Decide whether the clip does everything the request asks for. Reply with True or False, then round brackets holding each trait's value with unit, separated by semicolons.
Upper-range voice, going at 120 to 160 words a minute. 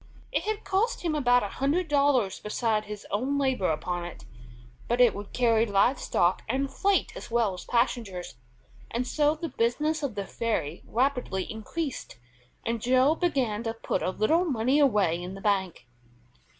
False (235 Hz; 170 wpm)